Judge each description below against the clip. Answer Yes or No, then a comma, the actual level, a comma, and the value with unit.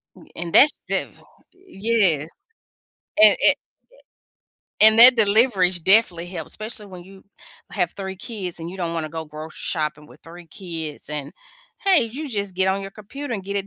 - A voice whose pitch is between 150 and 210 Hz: Yes, high, 190 Hz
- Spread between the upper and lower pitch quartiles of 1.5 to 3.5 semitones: No, average, 4.6 semitones